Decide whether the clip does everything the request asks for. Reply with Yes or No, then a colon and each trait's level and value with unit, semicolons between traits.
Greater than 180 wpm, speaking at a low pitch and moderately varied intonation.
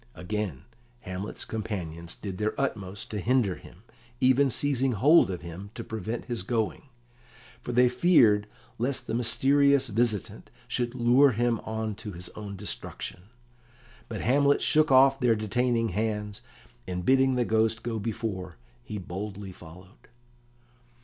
No: average, 140 wpm; low, 110 Hz; average, 3.9 semitones